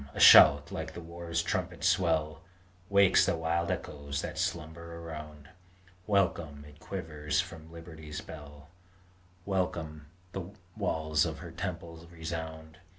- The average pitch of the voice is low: Yes, very low, 80 Hz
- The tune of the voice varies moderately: No, narrow, 2.0 semitones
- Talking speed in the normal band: No, slow, 125 wpm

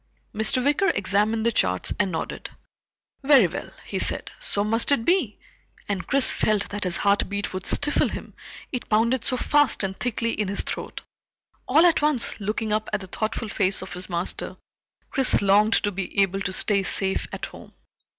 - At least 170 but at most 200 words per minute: Yes, average, 180 wpm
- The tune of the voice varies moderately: Yes, average, 4.1 semitones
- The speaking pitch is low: No, high, 210 Hz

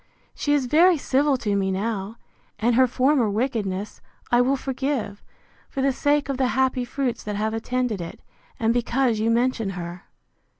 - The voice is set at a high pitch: Yes, high, 245 Hz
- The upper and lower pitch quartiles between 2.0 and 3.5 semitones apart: No, average, 3.9 semitones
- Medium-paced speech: Yes, average, 170 wpm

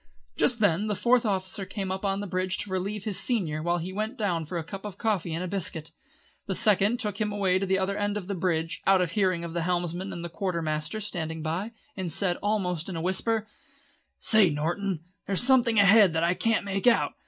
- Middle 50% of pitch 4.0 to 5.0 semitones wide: No, average, 3.2 semitones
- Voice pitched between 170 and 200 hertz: Yes, high, 190 Hz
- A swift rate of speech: Yes, fast, 235 wpm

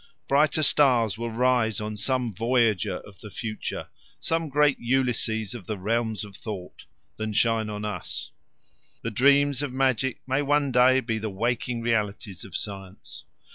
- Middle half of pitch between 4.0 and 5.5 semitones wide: No, average, 3.6 semitones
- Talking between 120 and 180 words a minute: Yes, average, 155 wpm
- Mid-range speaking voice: No, low, 115 Hz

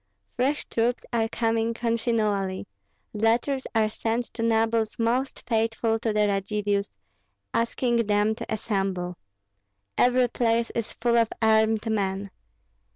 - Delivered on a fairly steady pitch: Yes, narrow, 1.7 semitones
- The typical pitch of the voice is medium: No, high, 225 Hz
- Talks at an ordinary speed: No, slow, 120 wpm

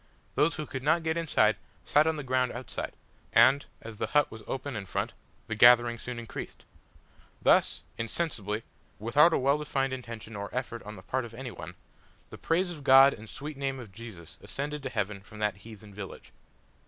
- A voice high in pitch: No, low, 125 Hz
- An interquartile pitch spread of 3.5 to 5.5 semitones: Yes, average, 4.5 semitones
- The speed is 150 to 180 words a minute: No, average, 195 wpm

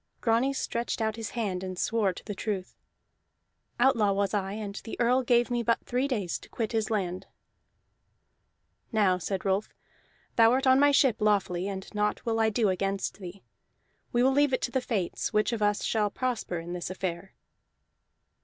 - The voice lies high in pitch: Yes, high, 215 Hz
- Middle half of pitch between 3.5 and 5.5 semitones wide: Yes, average, 3.8 semitones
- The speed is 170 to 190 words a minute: Yes, average, 180 wpm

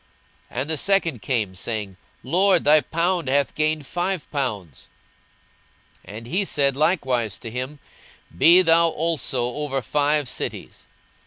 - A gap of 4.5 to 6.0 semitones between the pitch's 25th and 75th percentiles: Yes, average, 5.2 semitones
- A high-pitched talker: No, medium, 145 Hz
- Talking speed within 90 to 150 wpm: Yes, average, 140 wpm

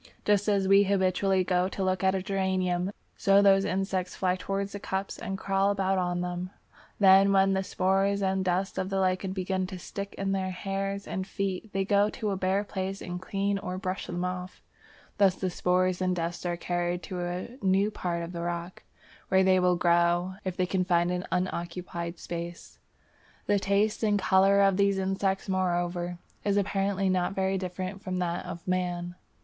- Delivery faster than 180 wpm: Yes, average, 190 wpm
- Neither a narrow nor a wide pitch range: No, narrow, 1.4 semitones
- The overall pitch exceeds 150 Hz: Yes, high, 190 Hz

